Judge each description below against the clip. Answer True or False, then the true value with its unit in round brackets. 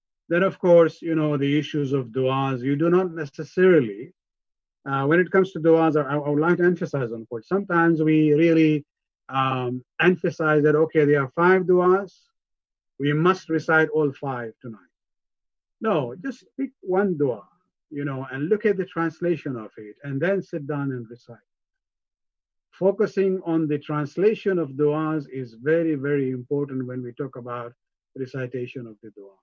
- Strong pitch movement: False (4.8 semitones)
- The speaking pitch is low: False (150 Hz)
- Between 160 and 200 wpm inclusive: True (165 wpm)